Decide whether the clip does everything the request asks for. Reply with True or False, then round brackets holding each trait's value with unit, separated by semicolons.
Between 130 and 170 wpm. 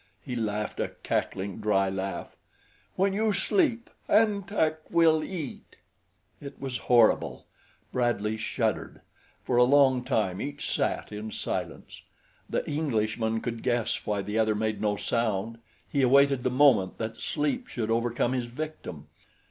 True (140 wpm)